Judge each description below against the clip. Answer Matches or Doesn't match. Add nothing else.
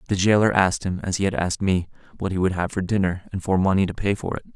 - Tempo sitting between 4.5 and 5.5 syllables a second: Doesn't match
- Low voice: Matches